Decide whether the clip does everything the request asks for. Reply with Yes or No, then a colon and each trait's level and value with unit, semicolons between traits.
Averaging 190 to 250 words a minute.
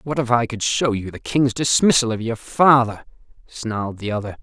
Yes: fast, 205 wpm